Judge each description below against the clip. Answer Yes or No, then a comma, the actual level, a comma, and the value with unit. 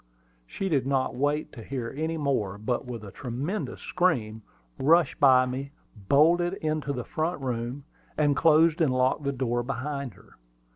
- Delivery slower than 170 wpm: Yes, average, 160 wpm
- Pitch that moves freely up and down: No, average, 3.8 semitones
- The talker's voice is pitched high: No, medium, 140 Hz